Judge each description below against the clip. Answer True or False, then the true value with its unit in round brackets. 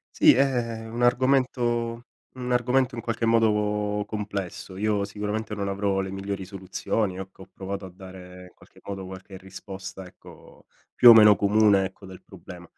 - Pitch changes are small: False (3.2 semitones)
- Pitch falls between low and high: False (105 Hz)